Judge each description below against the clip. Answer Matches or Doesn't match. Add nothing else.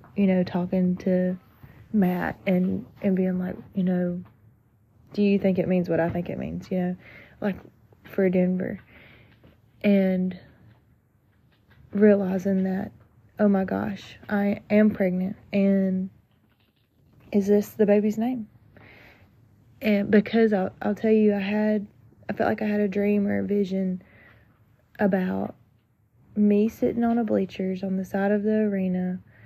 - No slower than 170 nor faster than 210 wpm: Doesn't match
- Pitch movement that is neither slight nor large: Doesn't match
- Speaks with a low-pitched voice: Doesn't match